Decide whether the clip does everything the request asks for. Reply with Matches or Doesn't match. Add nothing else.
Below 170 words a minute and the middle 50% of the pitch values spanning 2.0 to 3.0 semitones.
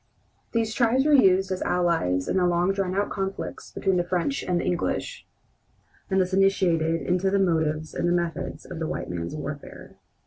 Doesn't match